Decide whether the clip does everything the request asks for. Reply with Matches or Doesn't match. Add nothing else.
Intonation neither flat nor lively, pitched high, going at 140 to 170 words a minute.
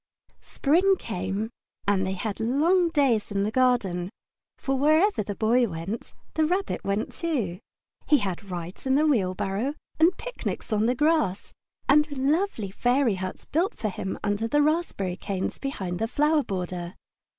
Doesn't match